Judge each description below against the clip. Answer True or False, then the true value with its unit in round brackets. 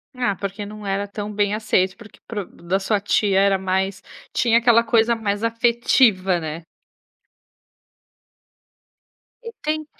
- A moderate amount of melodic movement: True (3.0 semitones)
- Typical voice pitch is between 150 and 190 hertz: False (205 Hz)